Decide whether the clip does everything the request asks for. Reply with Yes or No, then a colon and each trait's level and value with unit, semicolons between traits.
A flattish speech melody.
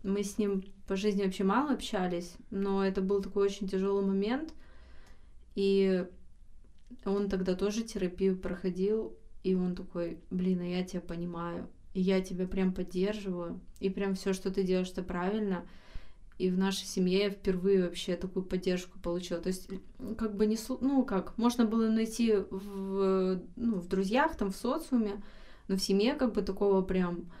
Yes: narrow, 1.8 semitones